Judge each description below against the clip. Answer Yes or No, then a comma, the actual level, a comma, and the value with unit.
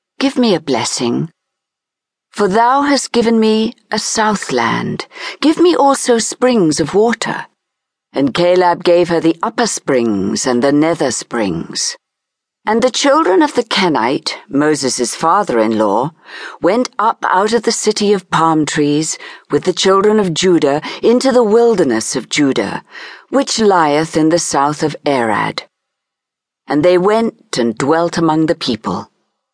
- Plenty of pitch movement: Yes, wide, 6.9 semitones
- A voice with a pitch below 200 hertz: Yes, medium, 185 Hz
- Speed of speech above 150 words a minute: No, average, 145 wpm